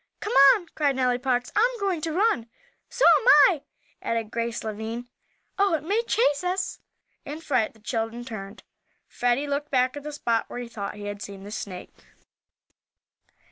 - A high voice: Yes, very high, 250 Hz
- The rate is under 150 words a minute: No, average, 175 wpm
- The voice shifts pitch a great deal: Yes, wide, 6.3 semitones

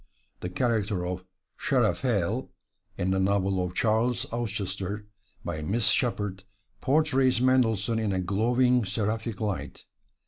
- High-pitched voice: No, low, 105 Hz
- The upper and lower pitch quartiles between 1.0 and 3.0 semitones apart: No, average, 3.9 semitones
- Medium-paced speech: No, slow, 115 wpm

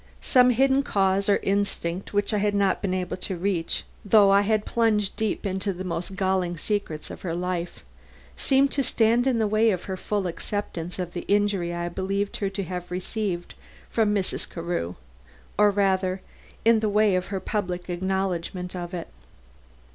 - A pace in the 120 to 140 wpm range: No, average, 180 wpm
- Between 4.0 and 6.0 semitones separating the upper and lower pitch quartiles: No, narrow, 2.6 semitones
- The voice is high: Yes, high, 195 Hz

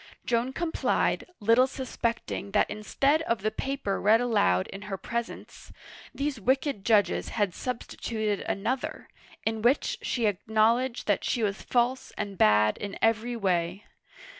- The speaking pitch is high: Yes, high, 225 Hz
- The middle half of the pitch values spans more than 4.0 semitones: No, average, 3.7 semitones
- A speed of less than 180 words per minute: Yes, average, 140 wpm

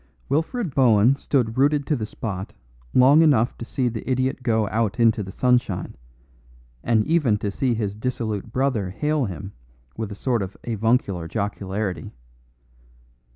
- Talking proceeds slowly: No, average, 150 wpm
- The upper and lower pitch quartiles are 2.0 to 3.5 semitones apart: No, average, 4.1 semitones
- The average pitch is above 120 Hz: No, low, 115 Hz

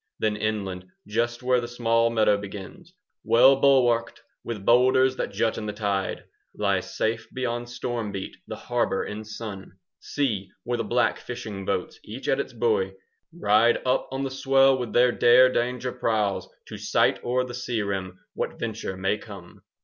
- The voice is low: Yes, low, 115 Hz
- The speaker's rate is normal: Yes, average, 170 wpm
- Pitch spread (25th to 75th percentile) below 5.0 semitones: Yes, average, 3.3 semitones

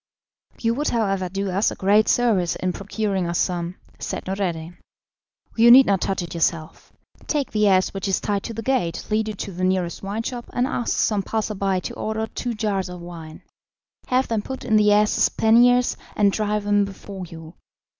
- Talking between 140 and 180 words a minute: No, average, 195 wpm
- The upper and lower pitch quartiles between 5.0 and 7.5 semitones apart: No, average, 3.2 semitones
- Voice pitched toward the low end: No, high, 200 Hz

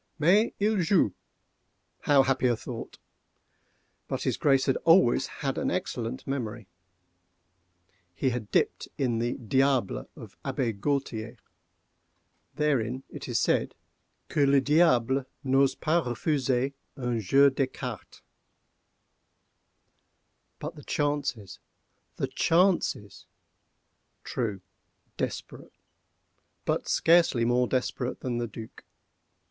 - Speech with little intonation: No, average, 3.3 semitones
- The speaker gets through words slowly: Yes, slow, 95 wpm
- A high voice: No, low, 130 Hz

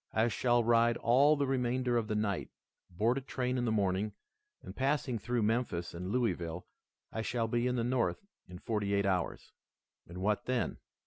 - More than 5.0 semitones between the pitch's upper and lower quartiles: No, average, 3.6 semitones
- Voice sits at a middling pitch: No, low, 115 Hz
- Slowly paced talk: No, average, 185 wpm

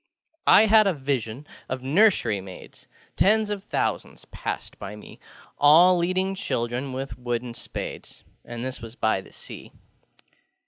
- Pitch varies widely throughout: Yes, wide, 7.7 semitones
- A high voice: No, low, 135 Hz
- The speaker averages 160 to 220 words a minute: No, average, 140 wpm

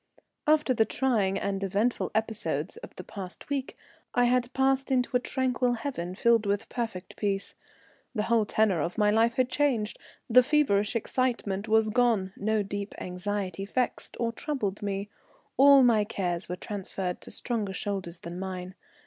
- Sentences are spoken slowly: No, average, 160 wpm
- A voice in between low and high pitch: No, high, 215 Hz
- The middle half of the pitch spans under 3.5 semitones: No, average, 4.0 semitones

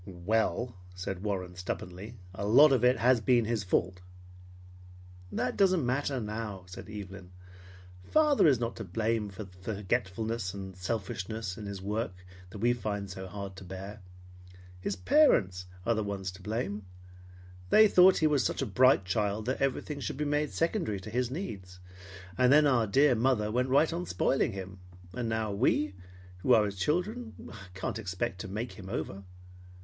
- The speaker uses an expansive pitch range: No, average, 4.9 semitones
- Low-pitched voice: Yes, low, 105 Hz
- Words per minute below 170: No, average, 175 wpm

